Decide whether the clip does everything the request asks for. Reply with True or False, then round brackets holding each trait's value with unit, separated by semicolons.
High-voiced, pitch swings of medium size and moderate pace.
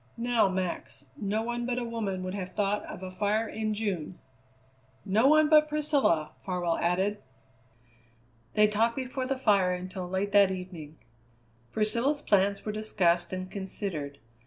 True (205 Hz; 4.0 semitones; 150 wpm)